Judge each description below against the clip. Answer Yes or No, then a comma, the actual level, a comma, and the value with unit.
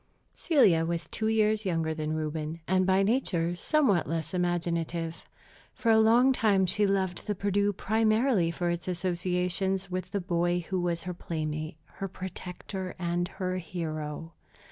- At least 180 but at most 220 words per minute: No, average, 150 wpm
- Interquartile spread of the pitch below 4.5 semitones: Yes, average, 2.8 semitones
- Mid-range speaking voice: Yes, medium, 180 Hz